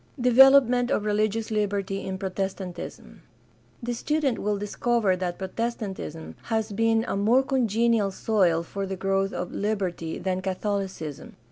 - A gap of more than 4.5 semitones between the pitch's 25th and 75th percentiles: No, average, 3.3 semitones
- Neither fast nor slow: No, slow, 130 wpm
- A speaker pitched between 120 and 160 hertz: No, high, 205 Hz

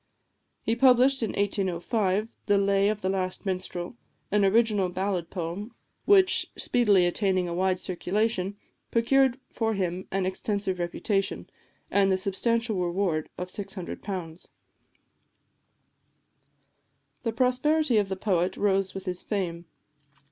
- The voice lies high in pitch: Yes, high, 195 Hz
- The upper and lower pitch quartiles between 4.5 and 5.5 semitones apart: No, average, 3.3 semitones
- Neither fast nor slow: No, slow, 120 wpm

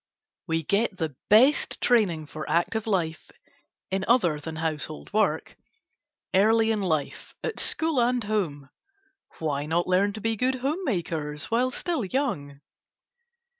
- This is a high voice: Yes, high, 195 Hz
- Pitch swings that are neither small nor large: No, wide, 6.7 semitones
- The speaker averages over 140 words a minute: No, slow, 135 wpm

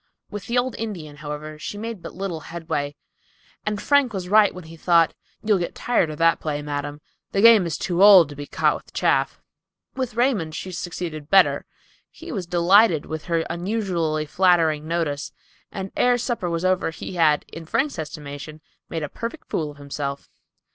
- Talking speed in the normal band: Yes, average, 180 wpm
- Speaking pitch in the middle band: Yes, medium, 170 Hz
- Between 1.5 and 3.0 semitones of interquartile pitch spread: No, average, 4.9 semitones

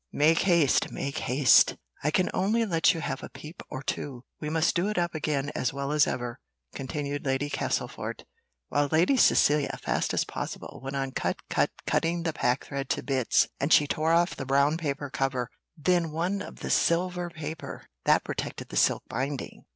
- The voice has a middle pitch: Yes, medium, 150 Hz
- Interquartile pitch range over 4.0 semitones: No, average, 3.5 semitones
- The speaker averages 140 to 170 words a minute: No, average, 180 wpm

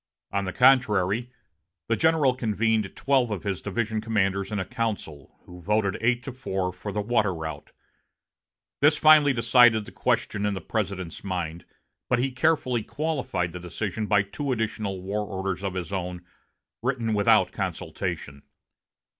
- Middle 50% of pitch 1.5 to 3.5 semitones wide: No, average, 4.3 semitones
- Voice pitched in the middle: No, low, 105 Hz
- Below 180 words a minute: Yes, average, 155 wpm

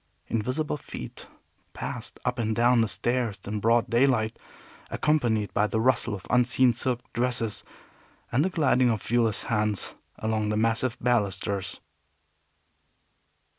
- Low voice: Yes, low, 115 Hz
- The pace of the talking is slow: Yes, slow, 130 wpm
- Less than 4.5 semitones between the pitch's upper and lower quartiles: Yes, narrow, 2.5 semitones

